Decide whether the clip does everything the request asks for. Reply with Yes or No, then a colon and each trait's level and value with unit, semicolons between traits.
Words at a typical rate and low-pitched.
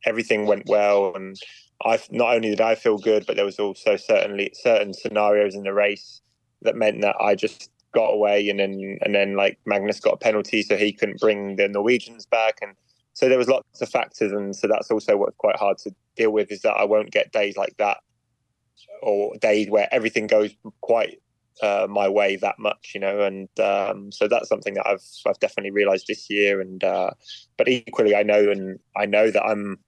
No: fast, 210 wpm; low, 105 Hz